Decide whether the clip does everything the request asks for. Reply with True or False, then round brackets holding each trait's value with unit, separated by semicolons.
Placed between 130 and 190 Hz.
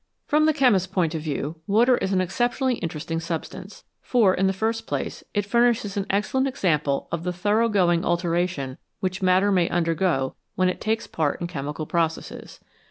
True (185 Hz)